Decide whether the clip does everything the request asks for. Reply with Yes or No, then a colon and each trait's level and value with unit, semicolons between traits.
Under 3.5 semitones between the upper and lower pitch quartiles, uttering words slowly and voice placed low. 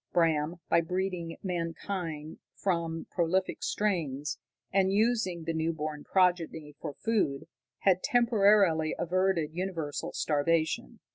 No: average, 3.1 semitones; slow, 110 wpm; medium, 170 Hz